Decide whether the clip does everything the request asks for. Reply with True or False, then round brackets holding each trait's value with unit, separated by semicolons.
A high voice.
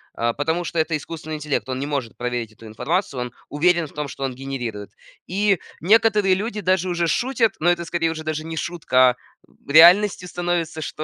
False (160 Hz)